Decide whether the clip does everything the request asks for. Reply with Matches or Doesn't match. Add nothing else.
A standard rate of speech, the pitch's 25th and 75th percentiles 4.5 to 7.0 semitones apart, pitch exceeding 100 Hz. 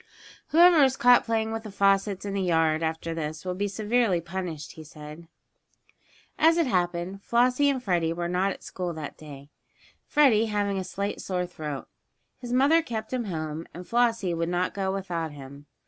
Matches